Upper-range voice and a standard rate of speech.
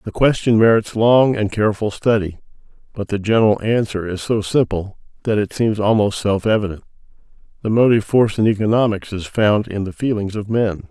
No: low, 105 Hz; average, 175 wpm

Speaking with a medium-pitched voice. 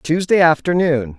Yes: medium, 160 Hz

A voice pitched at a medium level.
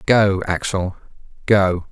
No: very low, 95 Hz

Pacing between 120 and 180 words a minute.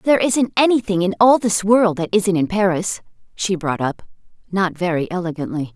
Yes: average, 175 wpm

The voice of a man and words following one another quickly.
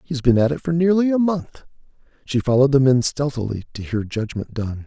Yes: male; fast, 210 wpm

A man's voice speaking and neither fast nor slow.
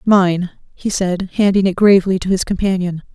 No: female; average, 170 wpm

